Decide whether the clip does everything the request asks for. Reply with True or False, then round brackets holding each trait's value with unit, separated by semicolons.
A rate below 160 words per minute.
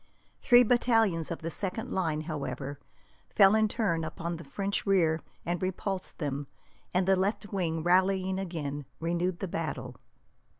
True (145 wpm)